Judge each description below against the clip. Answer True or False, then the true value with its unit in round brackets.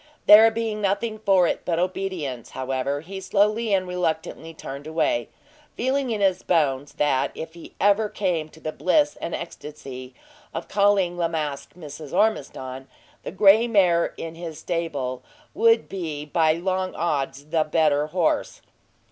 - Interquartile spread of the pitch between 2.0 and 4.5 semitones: False (4.9 semitones)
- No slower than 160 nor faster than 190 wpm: False (150 wpm)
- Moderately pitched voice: True (170 Hz)